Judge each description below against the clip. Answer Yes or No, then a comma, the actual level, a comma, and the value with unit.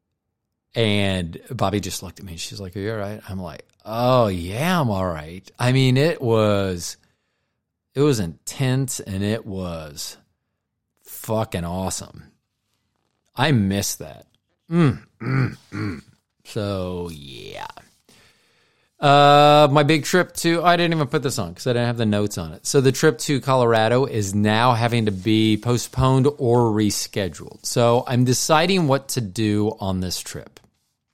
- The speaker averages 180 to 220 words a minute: No, average, 155 wpm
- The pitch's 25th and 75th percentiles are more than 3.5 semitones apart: Yes, average, 5.1 semitones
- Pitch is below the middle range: Yes, low, 115 Hz